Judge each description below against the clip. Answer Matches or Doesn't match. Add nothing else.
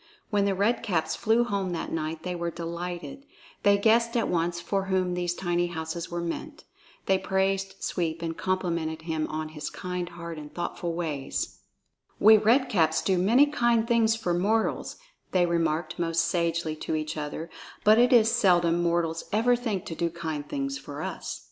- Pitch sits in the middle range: Matches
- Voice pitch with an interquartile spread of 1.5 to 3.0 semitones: Doesn't match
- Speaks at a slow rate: Doesn't match